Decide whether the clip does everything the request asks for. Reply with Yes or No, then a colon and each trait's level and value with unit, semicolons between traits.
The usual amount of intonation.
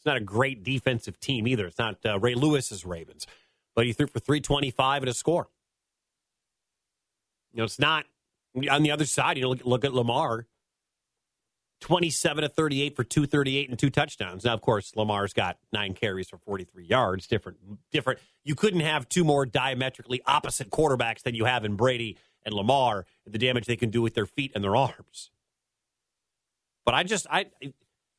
Yes: average, 4.4 semitones